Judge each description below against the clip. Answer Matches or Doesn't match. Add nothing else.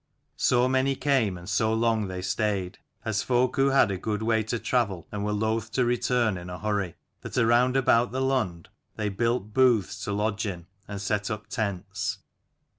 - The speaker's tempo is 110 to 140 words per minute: Doesn't match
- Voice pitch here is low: Matches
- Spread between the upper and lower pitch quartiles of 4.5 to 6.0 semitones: Doesn't match